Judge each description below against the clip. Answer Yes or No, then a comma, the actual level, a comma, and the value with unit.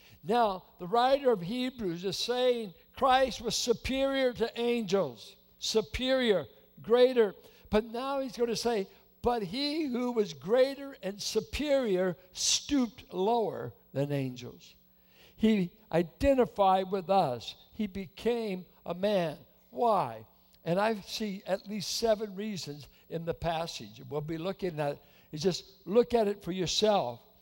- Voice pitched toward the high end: Yes, high, 205 Hz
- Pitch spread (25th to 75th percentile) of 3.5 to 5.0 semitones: No, wide, 5.4 semitones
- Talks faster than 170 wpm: No, slow, 135 wpm